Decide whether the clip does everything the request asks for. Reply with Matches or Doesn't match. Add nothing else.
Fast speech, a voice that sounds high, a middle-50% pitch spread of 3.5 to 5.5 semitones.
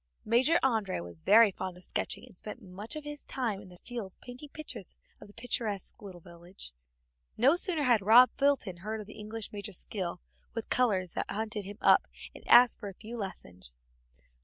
Doesn't match